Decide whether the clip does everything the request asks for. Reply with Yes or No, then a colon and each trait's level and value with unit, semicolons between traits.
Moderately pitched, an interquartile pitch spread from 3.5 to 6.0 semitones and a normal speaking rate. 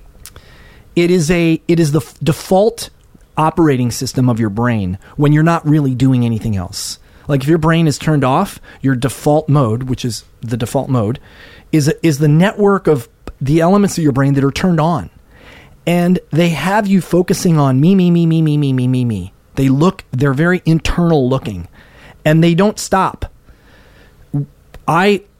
Yes: medium, 150 Hz; average, 4.7 semitones; average, 175 wpm